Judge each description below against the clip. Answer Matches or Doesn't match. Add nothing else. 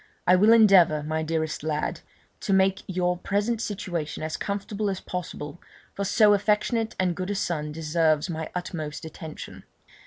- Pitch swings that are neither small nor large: Matches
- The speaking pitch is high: Doesn't match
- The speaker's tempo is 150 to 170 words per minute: Matches